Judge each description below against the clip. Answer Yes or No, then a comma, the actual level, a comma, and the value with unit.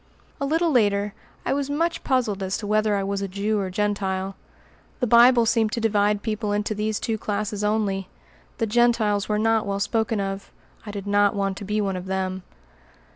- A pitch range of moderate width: No, narrow, 2.1 semitones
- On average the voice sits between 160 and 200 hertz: No, high, 210 Hz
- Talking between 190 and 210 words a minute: Yes, average, 195 wpm